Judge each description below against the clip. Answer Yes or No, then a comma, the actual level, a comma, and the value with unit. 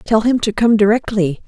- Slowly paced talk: No, fast, 205 wpm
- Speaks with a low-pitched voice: No, high, 215 Hz